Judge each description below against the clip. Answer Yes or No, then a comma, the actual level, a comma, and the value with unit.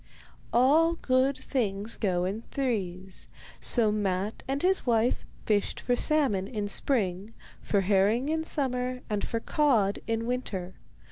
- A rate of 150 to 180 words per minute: No, slow, 135 wpm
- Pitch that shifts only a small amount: No, average, 4.8 semitones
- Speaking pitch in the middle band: No, high, 225 Hz